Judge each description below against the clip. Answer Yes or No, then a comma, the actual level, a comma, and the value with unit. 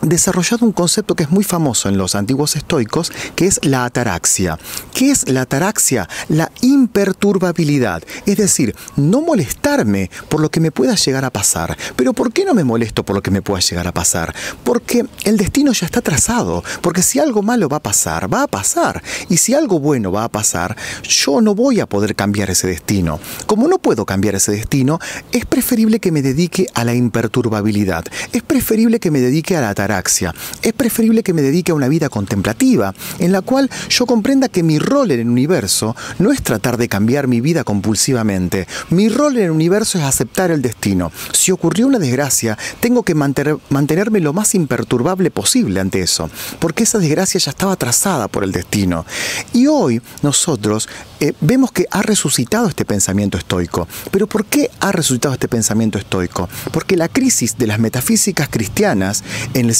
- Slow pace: No, fast, 190 wpm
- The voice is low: No, medium, 145 Hz